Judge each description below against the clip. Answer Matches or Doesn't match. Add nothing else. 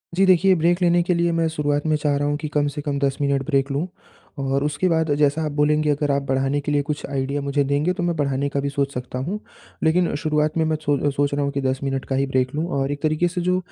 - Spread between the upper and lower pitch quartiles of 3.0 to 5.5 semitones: Doesn't match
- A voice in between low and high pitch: Matches